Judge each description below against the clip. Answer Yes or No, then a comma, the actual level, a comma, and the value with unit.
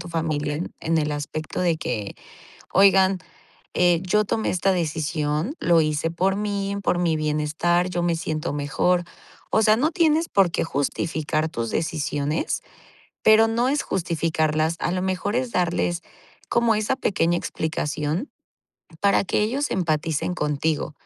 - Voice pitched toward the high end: No, medium, 170 Hz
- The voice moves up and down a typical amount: Yes, average, 4.1 semitones